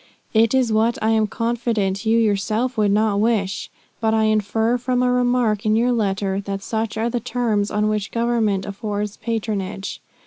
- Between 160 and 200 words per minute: Yes, average, 175 wpm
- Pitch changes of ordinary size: No, narrow, 2.3 semitones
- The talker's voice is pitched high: Yes, high, 220 Hz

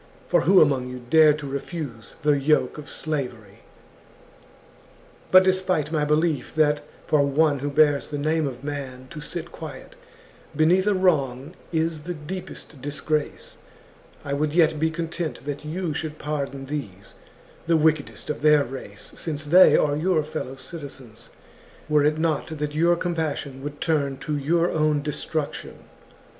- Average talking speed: Yes, average, 160 wpm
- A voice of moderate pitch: Yes, medium, 150 Hz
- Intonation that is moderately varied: No, narrow, 2.2 semitones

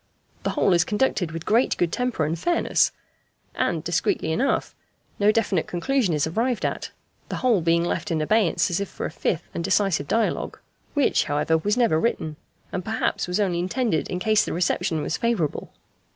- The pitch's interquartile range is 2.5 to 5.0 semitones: No, wide, 5.5 semitones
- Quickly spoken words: No, average, 180 wpm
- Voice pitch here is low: No, medium, 185 Hz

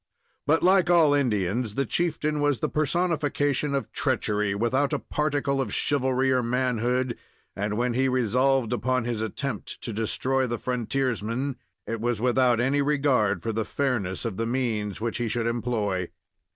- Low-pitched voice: Yes, low, 125 Hz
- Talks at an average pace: Yes, average, 160 wpm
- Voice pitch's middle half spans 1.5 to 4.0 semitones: Yes, average, 3.4 semitones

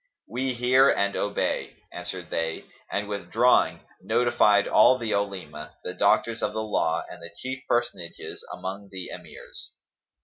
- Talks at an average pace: Yes, average, 145 wpm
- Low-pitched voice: Yes, low, 100 Hz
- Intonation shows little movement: No, average, 4.6 semitones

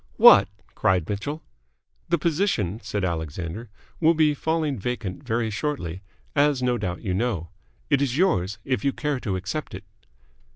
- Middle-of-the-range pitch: No, low, 115 Hz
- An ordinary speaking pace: Yes, average, 155 wpm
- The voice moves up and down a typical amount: No, wide, 7.7 semitones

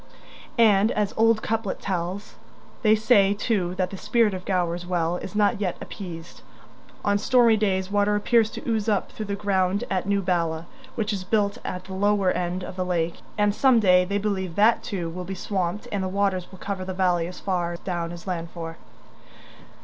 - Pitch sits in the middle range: No, high, 195 Hz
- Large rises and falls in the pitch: No, narrow, 2.5 semitones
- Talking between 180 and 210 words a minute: Yes, average, 195 wpm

